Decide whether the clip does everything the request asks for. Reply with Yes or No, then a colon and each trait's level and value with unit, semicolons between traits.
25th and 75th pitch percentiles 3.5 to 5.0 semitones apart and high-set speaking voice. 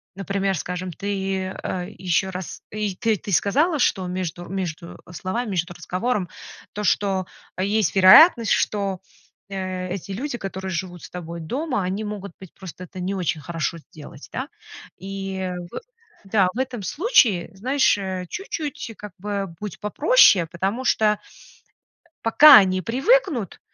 No: average, 2.9 semitones; high, 195 Hz